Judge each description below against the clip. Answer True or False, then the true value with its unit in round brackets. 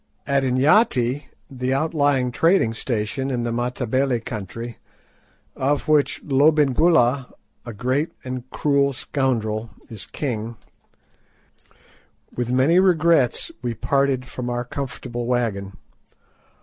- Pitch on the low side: True (130 Hz)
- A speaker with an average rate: False (105 wpm)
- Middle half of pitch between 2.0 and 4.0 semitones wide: True (2.9 semitones)